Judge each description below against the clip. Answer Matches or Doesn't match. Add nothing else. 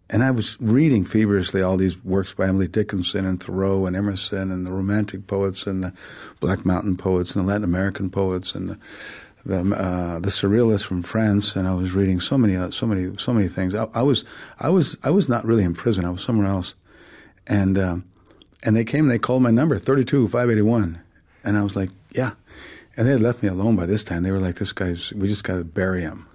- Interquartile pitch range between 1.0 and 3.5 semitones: Matches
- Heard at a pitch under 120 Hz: Matches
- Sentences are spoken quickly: Matches